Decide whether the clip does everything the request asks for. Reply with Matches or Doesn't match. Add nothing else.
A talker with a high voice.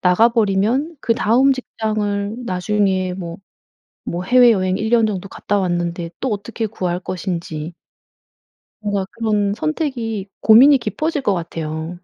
Matches